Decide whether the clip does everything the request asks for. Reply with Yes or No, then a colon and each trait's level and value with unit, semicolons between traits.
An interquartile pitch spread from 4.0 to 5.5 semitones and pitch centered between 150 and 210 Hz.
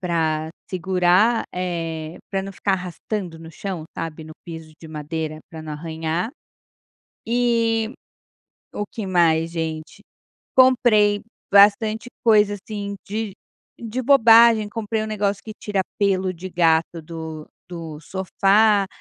Yes: average, 4.7 semitones; high, 190 Hz